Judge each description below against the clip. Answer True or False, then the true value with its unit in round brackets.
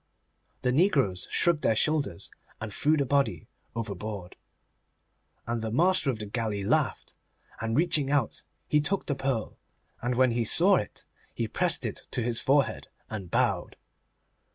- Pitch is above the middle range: False (125 Hz)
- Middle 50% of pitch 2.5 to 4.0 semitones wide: False (5.0 semitones)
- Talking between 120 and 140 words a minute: False (155 wpm)